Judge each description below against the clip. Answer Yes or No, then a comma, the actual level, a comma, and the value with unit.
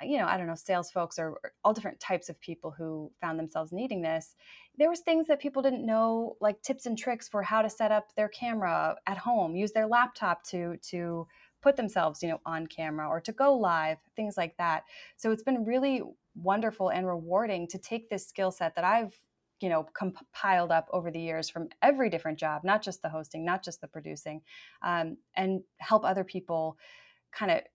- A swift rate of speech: Yes, fast, 210 wpm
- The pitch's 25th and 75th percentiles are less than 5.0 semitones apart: No, average, 5.3 semitones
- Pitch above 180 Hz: Yes, high, 190 Hz